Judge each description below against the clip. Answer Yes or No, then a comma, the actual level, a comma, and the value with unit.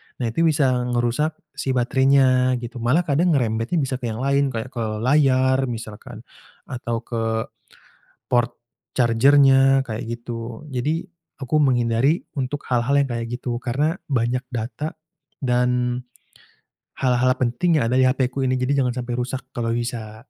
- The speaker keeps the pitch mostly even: Yes, narrow, 2.3 semitones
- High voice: No, low, 125 Hz